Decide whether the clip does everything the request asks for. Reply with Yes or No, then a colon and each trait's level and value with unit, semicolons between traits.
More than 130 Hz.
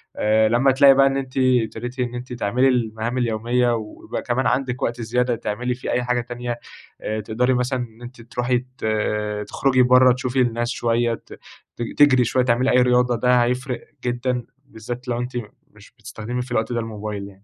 No: low, 125 Hz